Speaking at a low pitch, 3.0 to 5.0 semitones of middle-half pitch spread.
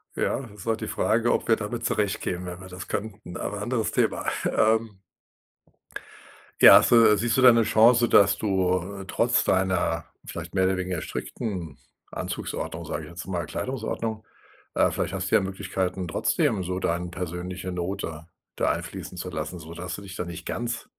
Yes: very low, 95 Hz; average, 3.5 semitones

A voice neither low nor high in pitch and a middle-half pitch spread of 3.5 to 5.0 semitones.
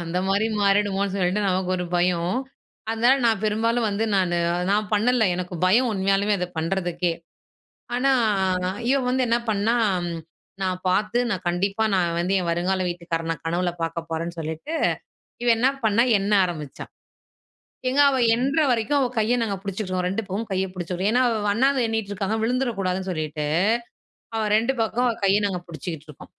No: high, 195 Hz; average, 4.0 semitones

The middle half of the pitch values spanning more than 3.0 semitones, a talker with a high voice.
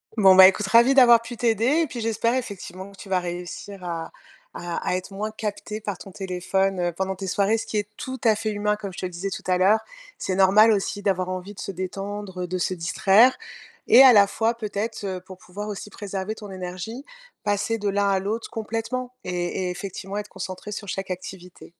No: average, 2.7 semitones; high, 200 Hz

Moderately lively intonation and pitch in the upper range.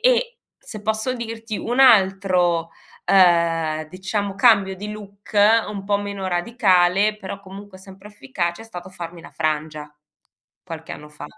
Yes: average, 3.4 semitones; high, 195 Hz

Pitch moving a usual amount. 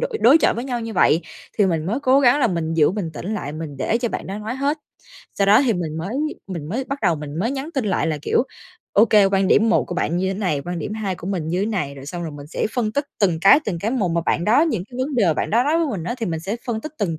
No: wide, 6.1 semitones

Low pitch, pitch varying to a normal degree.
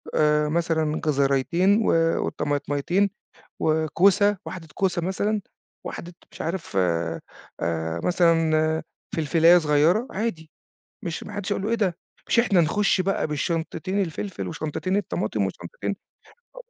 No: medium, 170 Hz; average, 4.1 semitones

